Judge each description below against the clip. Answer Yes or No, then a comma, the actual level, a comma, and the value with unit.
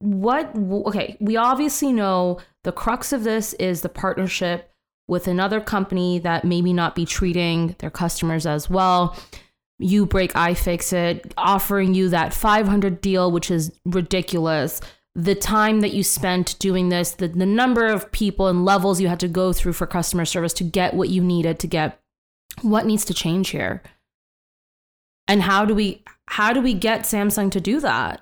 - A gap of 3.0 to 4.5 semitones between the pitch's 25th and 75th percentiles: No, narrow, 2.6 semitones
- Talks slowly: No, average, 175 wpm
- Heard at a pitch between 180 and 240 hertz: Yes, medium, 185 Hz